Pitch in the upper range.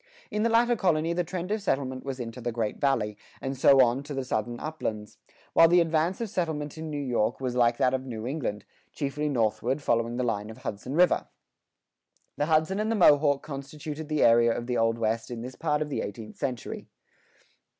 No: low, 135 Hz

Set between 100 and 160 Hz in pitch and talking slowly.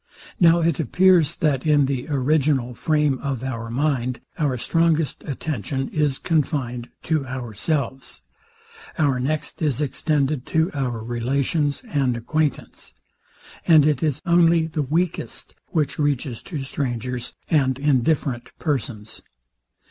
Yes: medium, 140 Hz; slow, 120 wpm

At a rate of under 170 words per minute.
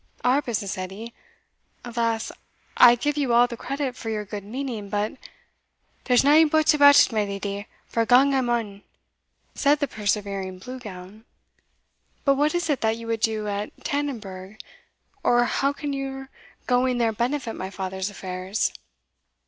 Yes: average, 155 wpm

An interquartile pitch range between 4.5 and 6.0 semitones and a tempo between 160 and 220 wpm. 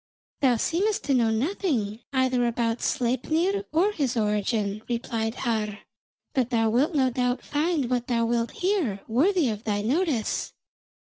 No: average, 5.0 semitones; average, 145 wpm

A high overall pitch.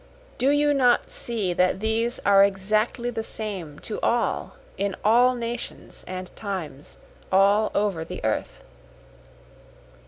Yes: high, 215 Hz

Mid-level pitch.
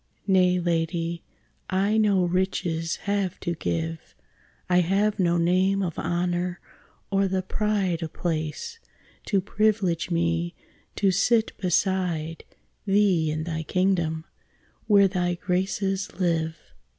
Yes: medium, 180 Hz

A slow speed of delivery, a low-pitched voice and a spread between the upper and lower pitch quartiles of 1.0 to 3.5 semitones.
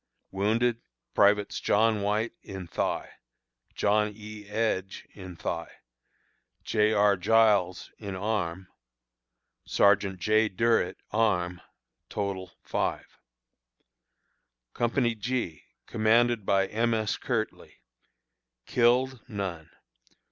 Yes: slow, 90 wpm; low, 105 Hz; average, 2.8 semitones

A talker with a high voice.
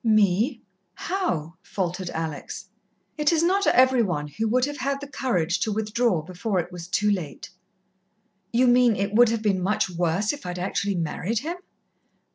Yes: high, 210 Hz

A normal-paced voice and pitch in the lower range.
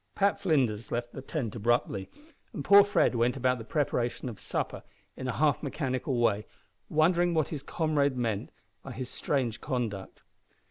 Yes: average, 165 wpm; low, 130 Hz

